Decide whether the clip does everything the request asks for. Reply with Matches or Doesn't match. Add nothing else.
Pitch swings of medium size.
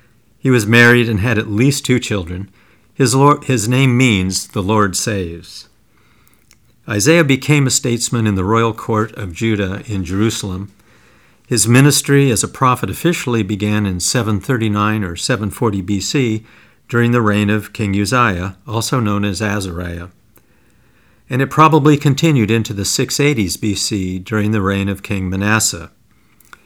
Matches